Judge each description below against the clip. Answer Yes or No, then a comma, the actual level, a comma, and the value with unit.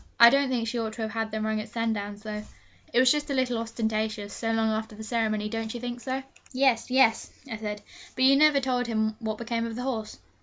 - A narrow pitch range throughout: Yes, narrow, 2.3 semitones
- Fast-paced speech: Yes, fast, 240 wpm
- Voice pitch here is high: Yes, high, 225 Hz